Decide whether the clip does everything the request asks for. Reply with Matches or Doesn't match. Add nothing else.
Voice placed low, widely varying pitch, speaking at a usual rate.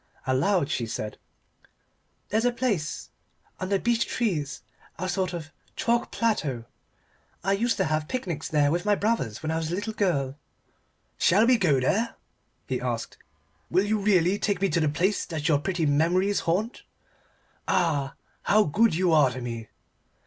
Doesn't match